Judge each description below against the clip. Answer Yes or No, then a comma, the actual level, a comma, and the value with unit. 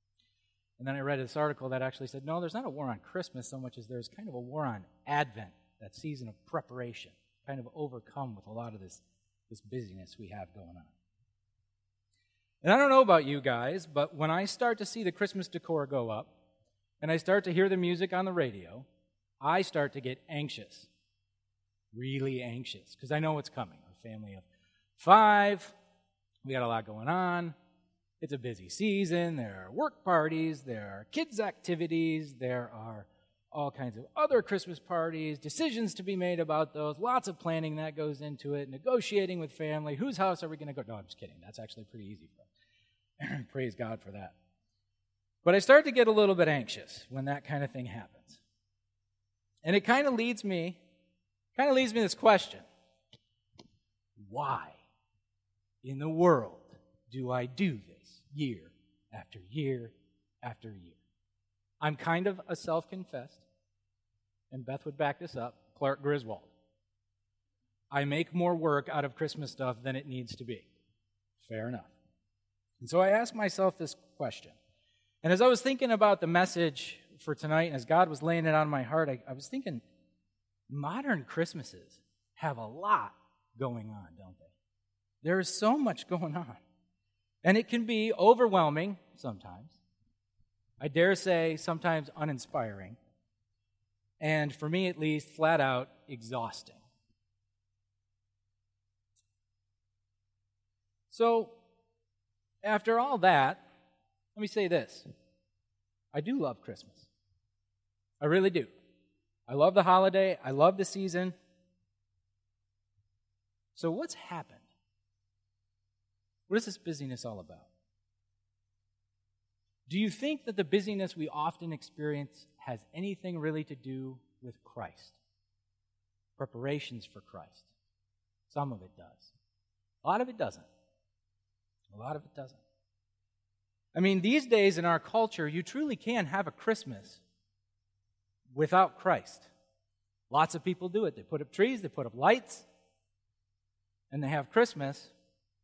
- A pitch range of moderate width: No, wide, 8.7 semitones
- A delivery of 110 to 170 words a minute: Yes, average, 155 wpm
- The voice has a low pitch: Yes, low, 125 Hz